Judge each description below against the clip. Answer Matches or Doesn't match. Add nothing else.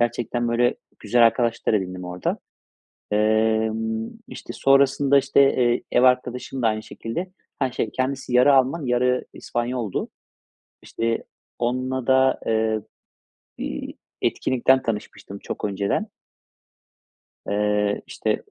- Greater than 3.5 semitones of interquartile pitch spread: Doesn't match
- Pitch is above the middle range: Doesn't match